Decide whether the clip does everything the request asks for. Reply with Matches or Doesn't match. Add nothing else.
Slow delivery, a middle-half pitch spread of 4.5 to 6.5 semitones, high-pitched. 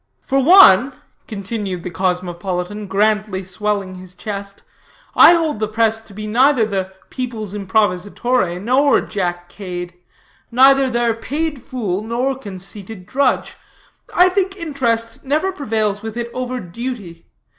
Matches